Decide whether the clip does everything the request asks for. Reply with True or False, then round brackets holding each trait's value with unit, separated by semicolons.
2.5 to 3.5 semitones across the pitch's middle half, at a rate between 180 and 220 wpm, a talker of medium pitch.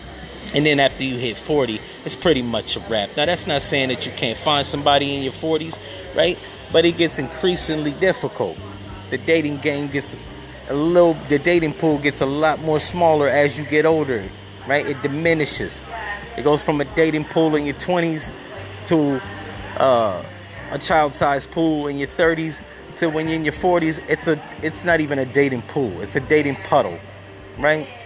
True (2.9 semitones; 185 wpm; 145 Hz)